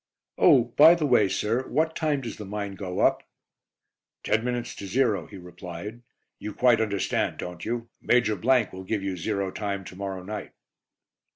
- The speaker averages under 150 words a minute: No, average, 170 wpm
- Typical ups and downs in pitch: Yes, average, 4.1 semitones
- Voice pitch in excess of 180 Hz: No, low, 105 Hz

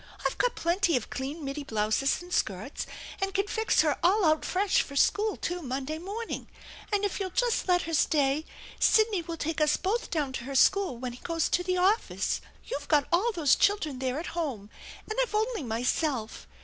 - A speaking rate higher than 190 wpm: Yes, average, 200 wpm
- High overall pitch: Yes, very high, 330 Hz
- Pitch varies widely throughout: Yes, wide, 6.3 semitones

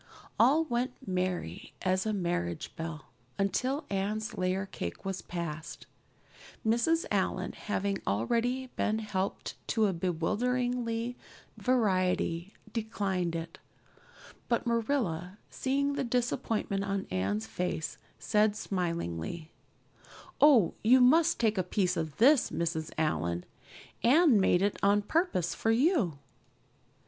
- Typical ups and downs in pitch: No, wide, 5.7 semitones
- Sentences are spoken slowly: Yes, slow, 115 wpm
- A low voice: No, high, 200 Hz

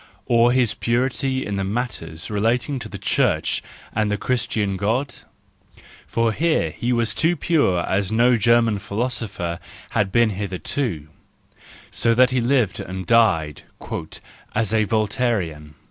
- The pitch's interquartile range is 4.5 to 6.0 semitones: No, average, 3.8 semitones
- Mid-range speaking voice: No, low, 110 Hz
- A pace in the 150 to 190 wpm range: No, slow, 135 wpm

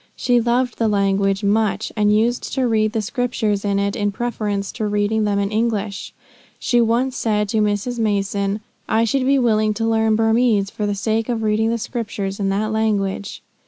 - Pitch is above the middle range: Yes, high, 215 Hz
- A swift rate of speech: No, average, 190 wpm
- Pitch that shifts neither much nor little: No, narrow, 2.1 semitones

